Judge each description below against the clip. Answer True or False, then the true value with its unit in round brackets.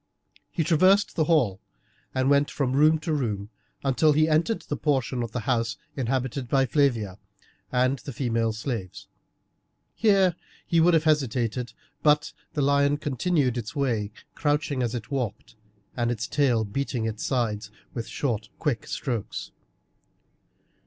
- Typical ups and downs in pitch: True (4.2 semitones)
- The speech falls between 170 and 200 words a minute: False (145 wpm)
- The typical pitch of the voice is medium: False (130 Hz)